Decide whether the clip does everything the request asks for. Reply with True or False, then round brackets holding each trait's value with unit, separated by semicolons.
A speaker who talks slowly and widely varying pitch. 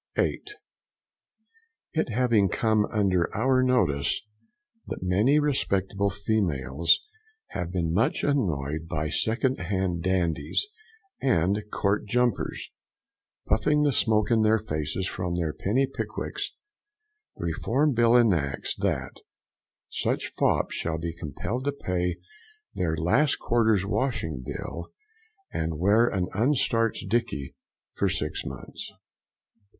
True (115 wpm; 5.8 semitones)